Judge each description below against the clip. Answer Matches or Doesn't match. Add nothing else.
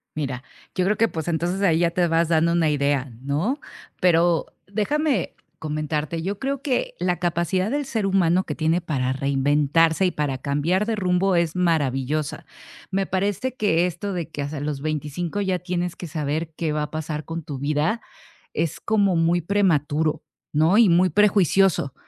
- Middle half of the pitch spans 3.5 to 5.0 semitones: Matches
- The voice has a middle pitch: Matches